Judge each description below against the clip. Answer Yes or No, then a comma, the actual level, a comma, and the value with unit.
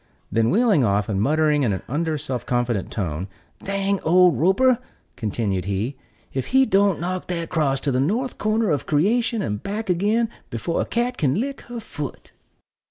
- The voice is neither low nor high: Yes, medium, 160 Hz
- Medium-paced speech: Yes, average, 175 wpm